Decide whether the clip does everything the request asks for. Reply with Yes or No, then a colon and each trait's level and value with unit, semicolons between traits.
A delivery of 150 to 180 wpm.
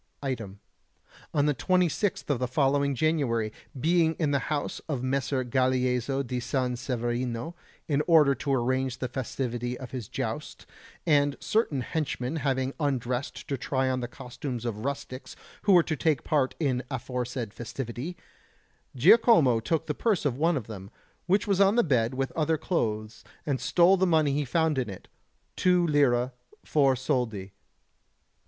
Yes: average, 160 wpm